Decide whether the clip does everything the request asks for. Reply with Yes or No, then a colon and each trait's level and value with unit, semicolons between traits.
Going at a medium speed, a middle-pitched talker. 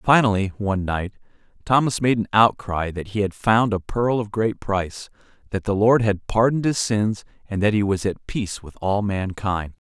No: average, 195 wpm; low, 105 Hz